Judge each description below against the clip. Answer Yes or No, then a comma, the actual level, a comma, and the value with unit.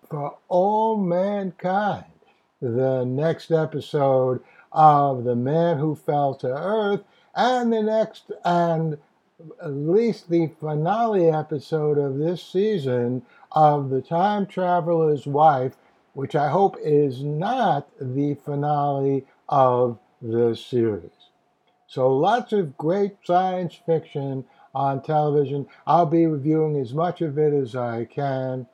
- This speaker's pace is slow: Yes, slow, 120 wpm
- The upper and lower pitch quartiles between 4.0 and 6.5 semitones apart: Yes, average, 4.3 semitones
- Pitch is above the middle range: No, medium, 150 Hz